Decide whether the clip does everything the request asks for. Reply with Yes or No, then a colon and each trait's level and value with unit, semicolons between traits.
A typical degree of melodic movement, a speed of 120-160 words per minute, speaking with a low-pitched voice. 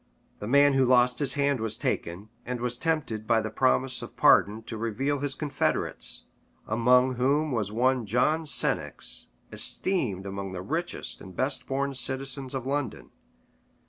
Yes: average, 3.9 semitones; average, 155 wpm; low, 125 Hz